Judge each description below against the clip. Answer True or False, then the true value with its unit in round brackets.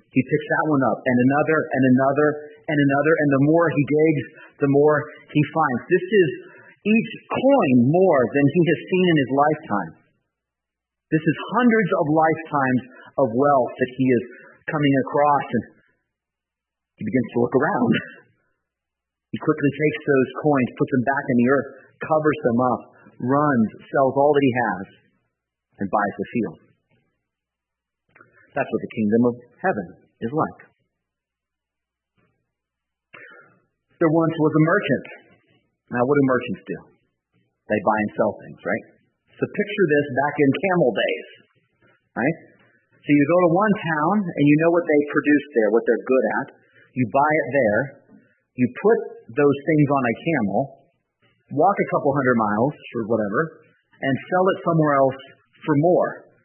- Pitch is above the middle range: False (145 Hz)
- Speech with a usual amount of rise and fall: True (4.1 semitones)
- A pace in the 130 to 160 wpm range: True (155 wpm)